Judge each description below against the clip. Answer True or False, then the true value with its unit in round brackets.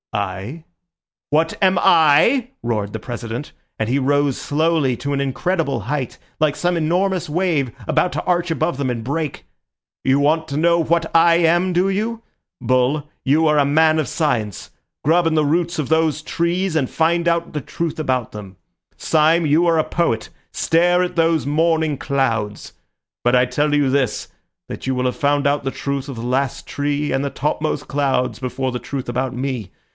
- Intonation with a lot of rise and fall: False (4.0 semitones)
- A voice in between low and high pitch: True (150 Hz)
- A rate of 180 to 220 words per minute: True (185 wpm)